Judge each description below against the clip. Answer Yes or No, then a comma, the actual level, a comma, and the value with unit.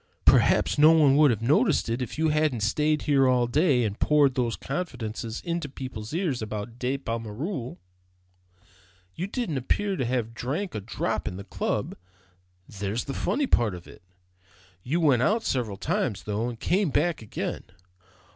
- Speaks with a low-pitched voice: Yes, low, 130 Hz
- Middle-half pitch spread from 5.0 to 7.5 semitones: Yes, average, 5.3 semitones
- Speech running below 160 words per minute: No, average, 165 wpm